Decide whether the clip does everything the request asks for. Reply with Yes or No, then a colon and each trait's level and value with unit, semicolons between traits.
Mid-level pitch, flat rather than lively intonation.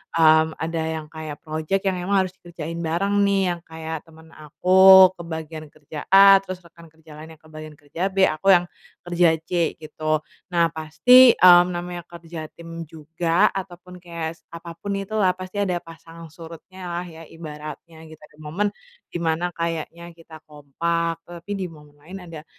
Yes: medium, 165 Hz; narrow, 2.2 semitones